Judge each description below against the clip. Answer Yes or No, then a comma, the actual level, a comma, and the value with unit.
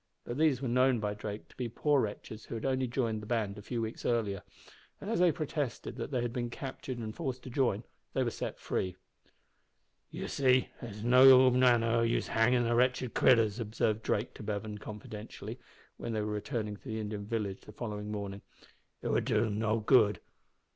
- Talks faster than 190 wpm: Yes, fast, 205 wpm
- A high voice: No, low, 115 Hz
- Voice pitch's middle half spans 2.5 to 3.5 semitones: Yes, average, 3.2 semitones